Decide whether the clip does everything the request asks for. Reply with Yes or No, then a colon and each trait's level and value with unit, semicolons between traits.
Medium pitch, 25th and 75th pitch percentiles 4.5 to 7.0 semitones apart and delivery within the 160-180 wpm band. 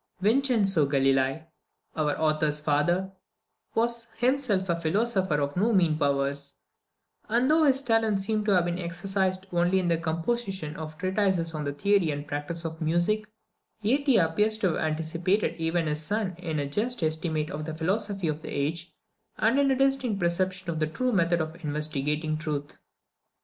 Yes: medium, 170 Hz; average, 5.1 semitones; average, 170 wpm